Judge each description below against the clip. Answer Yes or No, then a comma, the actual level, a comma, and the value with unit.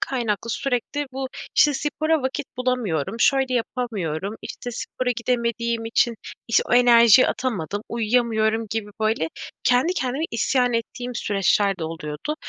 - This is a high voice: Yes, high, 235 Hz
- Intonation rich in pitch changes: No, average, 2.7 semitones